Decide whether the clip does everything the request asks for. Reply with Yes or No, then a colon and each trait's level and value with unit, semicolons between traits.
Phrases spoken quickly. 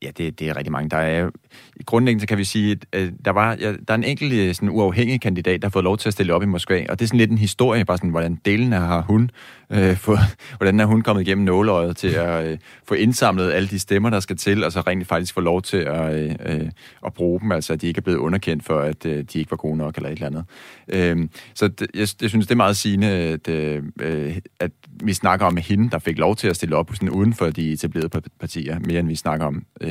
Yes: fast, 260 wpm